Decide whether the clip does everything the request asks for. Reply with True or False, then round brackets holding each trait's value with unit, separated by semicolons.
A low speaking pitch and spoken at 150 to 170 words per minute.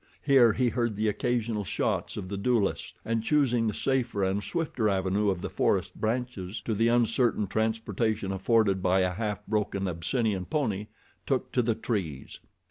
True (110 Hz; 165 wpm)